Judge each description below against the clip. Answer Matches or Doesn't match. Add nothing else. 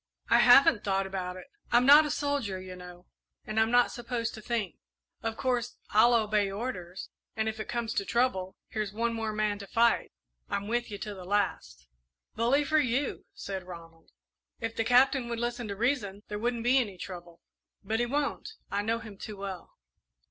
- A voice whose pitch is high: Matches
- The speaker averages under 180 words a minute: Doesn't match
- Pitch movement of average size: Matches